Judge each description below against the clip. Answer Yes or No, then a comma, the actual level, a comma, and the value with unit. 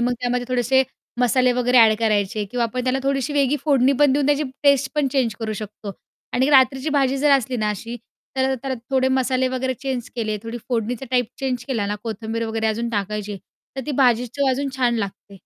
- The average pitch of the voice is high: Yes, very high, 250 Hz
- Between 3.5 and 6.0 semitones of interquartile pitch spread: No, average, 2.9 semitones